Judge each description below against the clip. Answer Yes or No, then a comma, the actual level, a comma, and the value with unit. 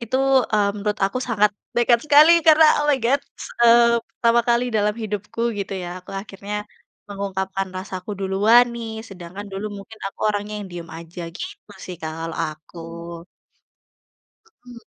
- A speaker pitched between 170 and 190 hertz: No, high, 210 Hz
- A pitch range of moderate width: Yes, average, 3.5 semitones